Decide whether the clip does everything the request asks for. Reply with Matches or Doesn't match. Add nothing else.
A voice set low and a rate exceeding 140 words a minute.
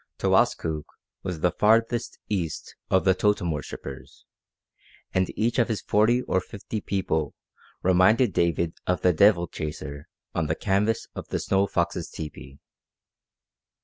Doesn't match